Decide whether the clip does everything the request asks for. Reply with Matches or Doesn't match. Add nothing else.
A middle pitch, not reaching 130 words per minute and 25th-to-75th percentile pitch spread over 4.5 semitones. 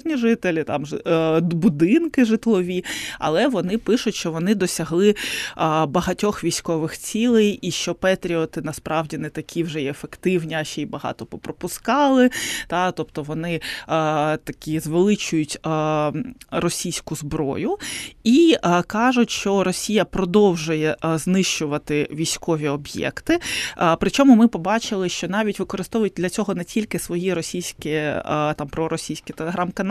Matches